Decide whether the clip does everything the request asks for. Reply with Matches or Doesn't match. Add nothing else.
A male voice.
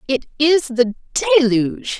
Doesn't match